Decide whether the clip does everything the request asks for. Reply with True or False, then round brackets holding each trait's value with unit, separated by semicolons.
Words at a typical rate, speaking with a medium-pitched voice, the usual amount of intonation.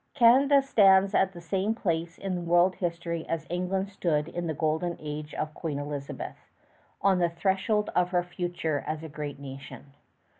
True (175 wpm; 175 Hz; 3.6 semitones)